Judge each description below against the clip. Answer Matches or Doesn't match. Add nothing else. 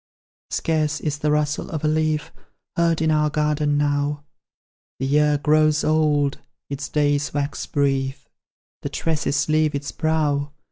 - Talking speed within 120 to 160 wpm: Matches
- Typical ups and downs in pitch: Doesn't match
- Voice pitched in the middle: Matches